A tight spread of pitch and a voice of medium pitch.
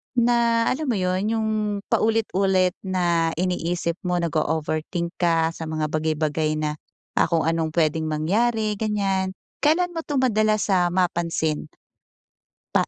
No: average, 5.0 semitones; medium, 180 Hz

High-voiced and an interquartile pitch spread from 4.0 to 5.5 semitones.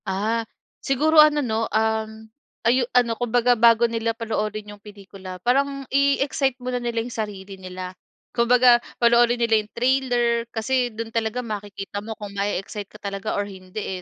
No: high, 230 Hz; average, 2.9 semitones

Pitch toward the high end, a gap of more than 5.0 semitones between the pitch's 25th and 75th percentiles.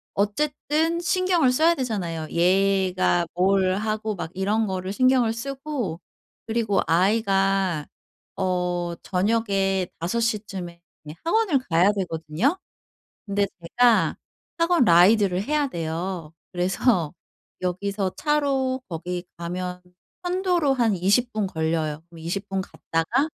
Yes: high, 195 Hz; wide, 5.6 semitones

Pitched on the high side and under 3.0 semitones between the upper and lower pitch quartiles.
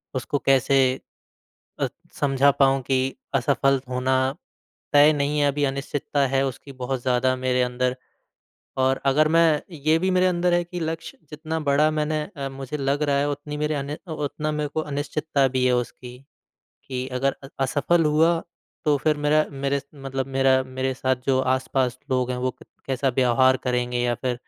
No: medium, 140 Hz; narrow, 2.5 semitones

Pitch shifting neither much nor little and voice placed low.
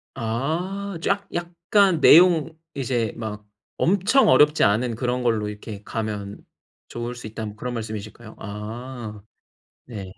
No: wide, 7.3 semitones; low, 120 Hz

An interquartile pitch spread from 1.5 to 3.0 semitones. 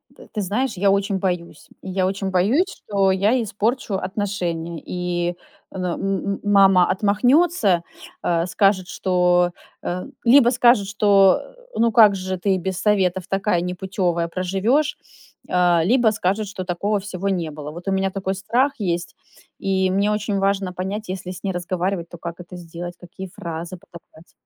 Yes: narrow, 2.4 semitones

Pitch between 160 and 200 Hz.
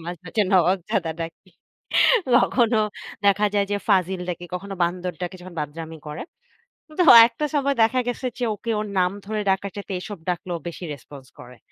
Yes: medium, 185 Hz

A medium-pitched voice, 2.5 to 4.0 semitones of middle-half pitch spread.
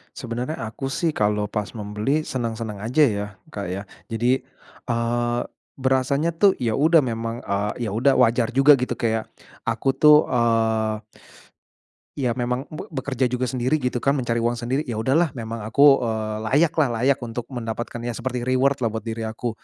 No: low, 120 Hz; average, 3.0 semitones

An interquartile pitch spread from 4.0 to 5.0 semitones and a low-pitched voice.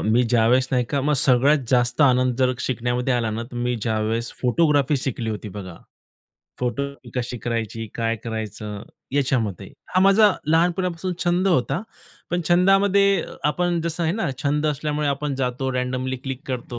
Yes: average, 4.6 semitones; low, 130 Hz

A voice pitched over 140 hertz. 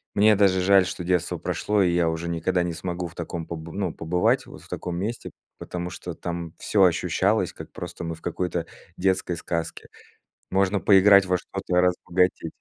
No: very low, 90 Hz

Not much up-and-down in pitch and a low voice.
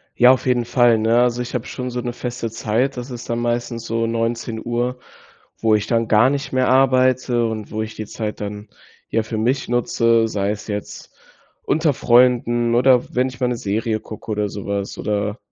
Yes: narrow, 2.1 semitones; low, 120 Hz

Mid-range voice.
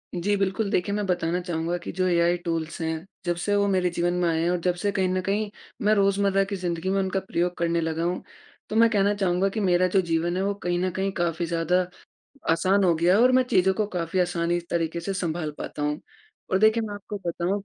Yes: medium, 180 Hz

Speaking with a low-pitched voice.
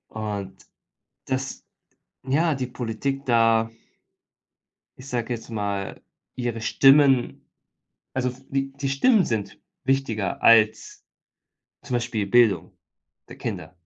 Yes: low, 120 Hz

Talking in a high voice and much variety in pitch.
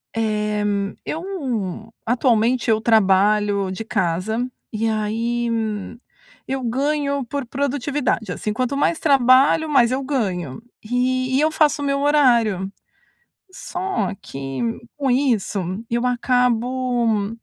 No: high, 240 Hz; average, 4.3 semitones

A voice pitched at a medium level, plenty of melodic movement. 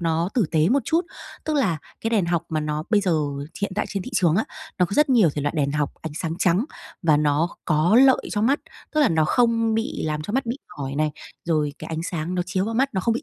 Yes: medium, 175 Hz; wide, 6.6 semitones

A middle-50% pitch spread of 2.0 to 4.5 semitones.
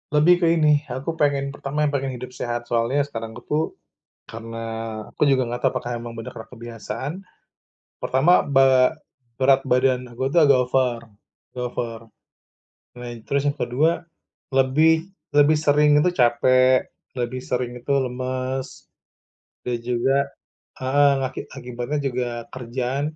Yes: narrow, 2.6 semitones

